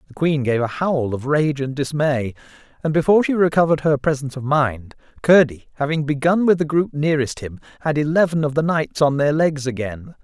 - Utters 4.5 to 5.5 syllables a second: No, 5.7 syllables/s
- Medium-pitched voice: Yes, medium, 145 Hz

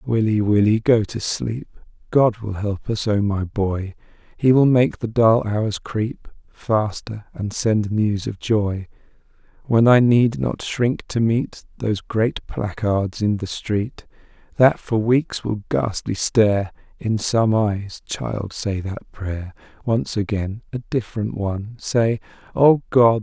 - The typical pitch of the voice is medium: No, low, 110 Hz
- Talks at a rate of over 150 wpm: No, average, 145 wpm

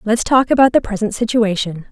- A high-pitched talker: Yes, high, 220 Hz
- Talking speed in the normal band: Yes, average, 190 wpm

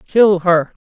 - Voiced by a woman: No, male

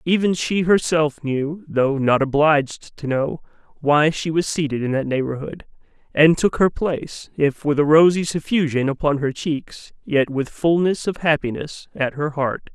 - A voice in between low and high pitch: Yes, medium, 150 Hz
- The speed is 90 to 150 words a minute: No, average, 170 wpm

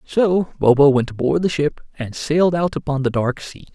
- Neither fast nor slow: No, fast, 210 wpm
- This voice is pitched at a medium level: Yes, medium, 150 Hz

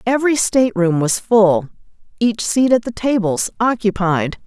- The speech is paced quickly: No, slow, 135 wpm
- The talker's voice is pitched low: No, high, 215 Hz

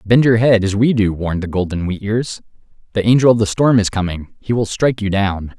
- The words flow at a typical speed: No, fast, 245 wpm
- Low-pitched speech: Yes, low, 105 Hz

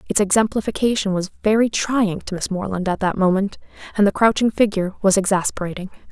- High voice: Yes, high, 200 Hz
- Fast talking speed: No, average, 165 wpm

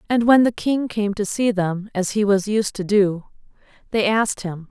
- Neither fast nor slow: No, fast, 215 wpm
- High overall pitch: Yes, high, 205 Hz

